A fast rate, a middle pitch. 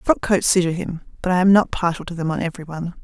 Yes: fast, 275 wpm; medium, 175 Hz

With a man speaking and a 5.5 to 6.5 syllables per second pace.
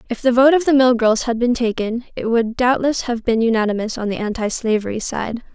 No: female; 5.6 syllables/s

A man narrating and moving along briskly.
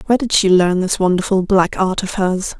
No: female; fast, 230 wpm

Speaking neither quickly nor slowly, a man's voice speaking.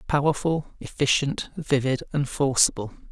No: slow, 95 wpm; male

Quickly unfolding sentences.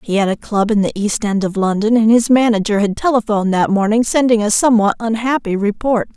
Yes: fast, 215 wpm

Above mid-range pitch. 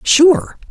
Yes: high, 220 Hz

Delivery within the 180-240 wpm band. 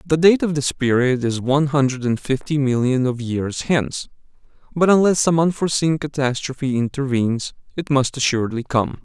No: average, 160 wpm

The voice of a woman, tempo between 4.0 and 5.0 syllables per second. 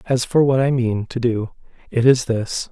No: male; 4.6 syllables/s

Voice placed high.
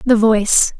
Yes: high, 220 Hz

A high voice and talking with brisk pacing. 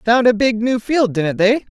Yes: high, 230 Hz; fast, 240 wpm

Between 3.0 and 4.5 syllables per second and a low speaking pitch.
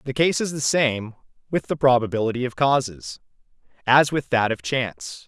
No: 5.1 syllables/s; low, 120 Hz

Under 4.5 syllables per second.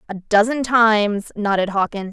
No: 4.7 syllables/s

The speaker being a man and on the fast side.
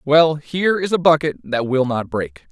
Yes: male; fast, 215 wpm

